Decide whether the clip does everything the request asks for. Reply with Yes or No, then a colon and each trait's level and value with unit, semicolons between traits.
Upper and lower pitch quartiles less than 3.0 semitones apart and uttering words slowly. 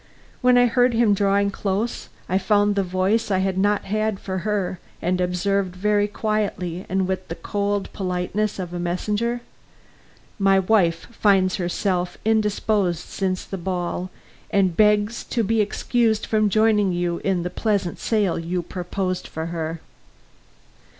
No: narrow, 2.6 semitones; average, 150 wpm